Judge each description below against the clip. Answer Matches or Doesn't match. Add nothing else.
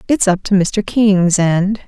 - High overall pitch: Matches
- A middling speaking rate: Matches